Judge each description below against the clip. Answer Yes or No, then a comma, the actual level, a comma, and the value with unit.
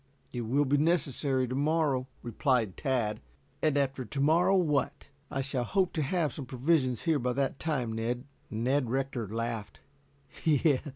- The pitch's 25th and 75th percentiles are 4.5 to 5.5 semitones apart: No, average, 3.5 semitones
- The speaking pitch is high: No, low, 135 Hz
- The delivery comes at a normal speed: Yes, average, 155 wpm